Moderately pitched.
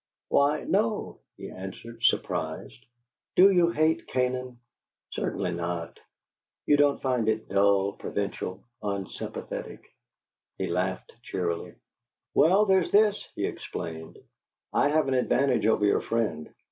No: low, 115 Hz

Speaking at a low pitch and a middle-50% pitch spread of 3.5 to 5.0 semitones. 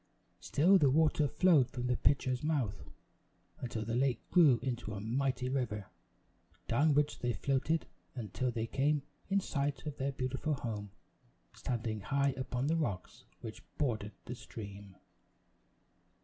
Yes: low, 130 Hz; average, 3.9 semitones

